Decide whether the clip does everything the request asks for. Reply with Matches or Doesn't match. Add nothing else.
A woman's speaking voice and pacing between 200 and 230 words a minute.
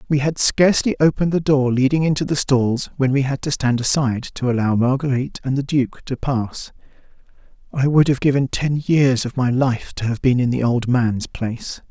Doesn't match